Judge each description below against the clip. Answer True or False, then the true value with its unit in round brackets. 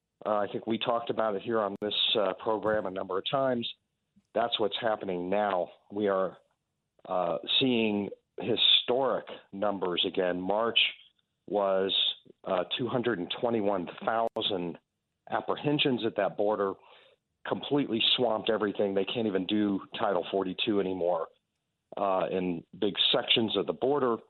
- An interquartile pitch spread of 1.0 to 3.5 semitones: True (3.0 semitones)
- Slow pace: True (130 wpm)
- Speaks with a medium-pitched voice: False (105 Hz)